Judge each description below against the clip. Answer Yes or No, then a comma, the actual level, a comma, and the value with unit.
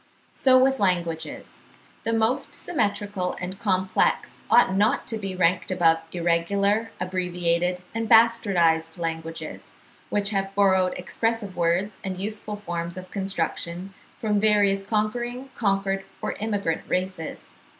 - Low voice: No, high, 195 Hz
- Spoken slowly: Yes, slow, 120 wpm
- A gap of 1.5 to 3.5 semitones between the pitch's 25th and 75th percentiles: Yes, average, 3.1 semitones